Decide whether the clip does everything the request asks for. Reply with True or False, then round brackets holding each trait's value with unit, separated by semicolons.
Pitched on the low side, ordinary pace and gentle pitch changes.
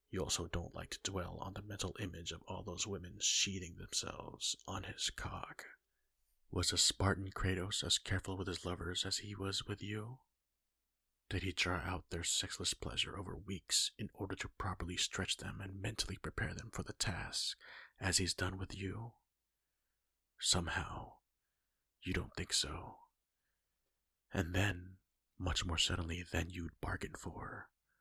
True (95 Hz; 160 wpm; 2.0 semitones)